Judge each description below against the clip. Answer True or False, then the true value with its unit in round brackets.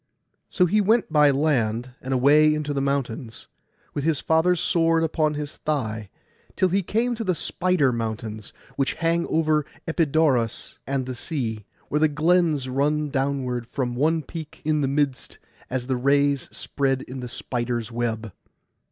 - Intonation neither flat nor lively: True (4.2 semitones)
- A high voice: False (140 Hz)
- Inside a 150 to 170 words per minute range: True (160 wpm)